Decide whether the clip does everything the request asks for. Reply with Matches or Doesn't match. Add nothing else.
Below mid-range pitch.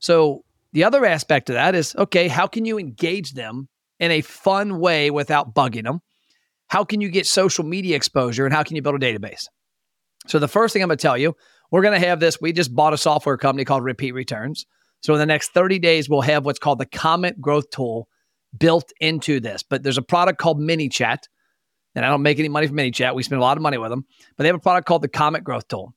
Doesn't match